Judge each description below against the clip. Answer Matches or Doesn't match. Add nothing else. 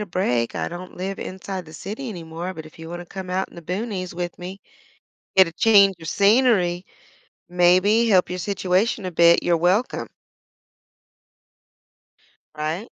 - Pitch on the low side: Doesn't match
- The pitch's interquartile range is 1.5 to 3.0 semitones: Matches